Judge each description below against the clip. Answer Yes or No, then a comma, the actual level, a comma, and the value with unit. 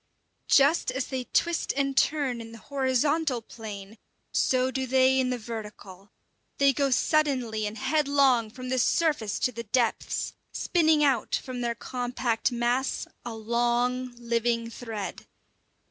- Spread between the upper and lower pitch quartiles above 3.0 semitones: No, average, 2.7 semitones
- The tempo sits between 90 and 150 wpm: Yes, average, 140 wpm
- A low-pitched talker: No, very high, 250 Hz